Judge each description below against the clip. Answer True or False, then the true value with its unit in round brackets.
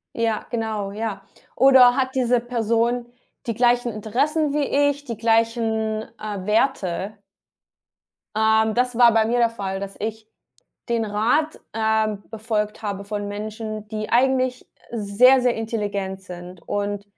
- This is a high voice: True (220 Hz)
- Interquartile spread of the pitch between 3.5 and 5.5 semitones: False (2.5 semitones)